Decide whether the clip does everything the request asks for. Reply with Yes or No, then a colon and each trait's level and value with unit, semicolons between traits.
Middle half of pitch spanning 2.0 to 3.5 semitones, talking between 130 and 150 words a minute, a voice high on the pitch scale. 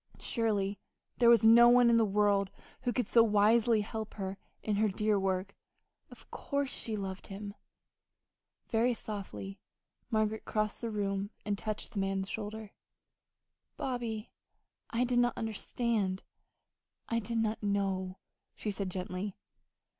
Yes: narrow, 2.5 semitones; average, 140 wpm; high, 215 Hz